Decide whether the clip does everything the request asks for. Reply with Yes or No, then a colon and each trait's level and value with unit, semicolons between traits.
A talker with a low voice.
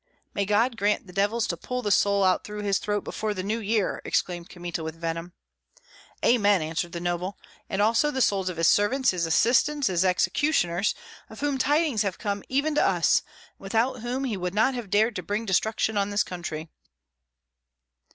No: high, 205 Hz